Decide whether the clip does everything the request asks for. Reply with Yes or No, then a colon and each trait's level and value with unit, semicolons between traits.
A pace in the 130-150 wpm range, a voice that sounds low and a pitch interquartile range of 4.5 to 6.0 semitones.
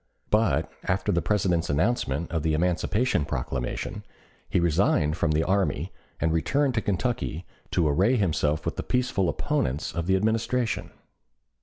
Yes: average, 145 wpm; very low, 90 Hz; average, 5.1 semitones